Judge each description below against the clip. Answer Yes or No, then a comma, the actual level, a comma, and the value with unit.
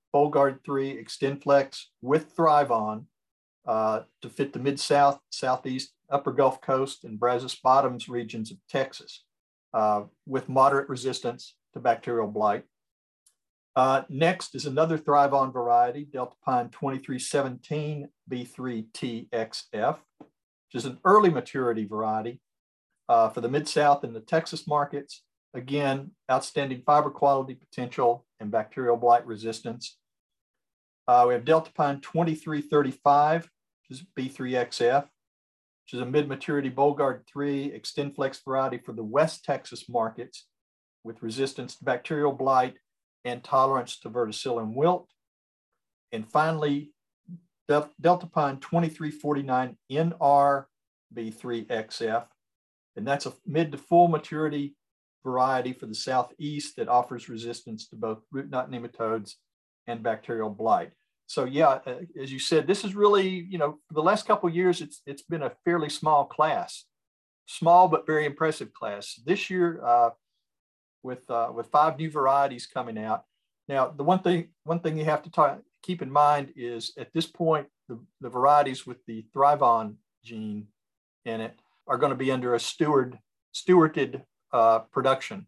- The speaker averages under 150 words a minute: Yes, average, 140 wpm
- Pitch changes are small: No, average, 3.8 semitones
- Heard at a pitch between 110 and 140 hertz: Yes, low, 135 Hz